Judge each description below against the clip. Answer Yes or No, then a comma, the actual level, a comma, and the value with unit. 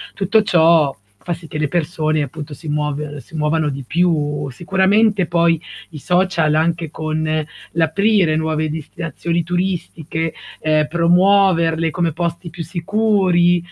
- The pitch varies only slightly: Yes, narrow, 2.3 semitones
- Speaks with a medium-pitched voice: Yes, medium, 165 Hz